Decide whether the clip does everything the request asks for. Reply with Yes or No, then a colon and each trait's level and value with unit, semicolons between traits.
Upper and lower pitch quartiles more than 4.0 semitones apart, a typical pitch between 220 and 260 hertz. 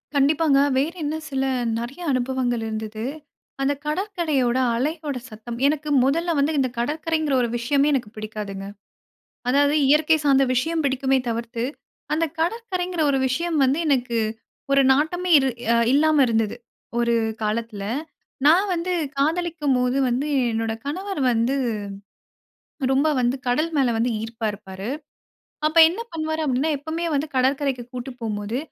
No: average, 4.7 semitones; very high, 275 Hz